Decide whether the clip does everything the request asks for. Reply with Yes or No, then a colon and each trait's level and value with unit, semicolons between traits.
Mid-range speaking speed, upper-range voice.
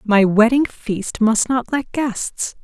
Yes: average, 160 wpm; high, 230 Hz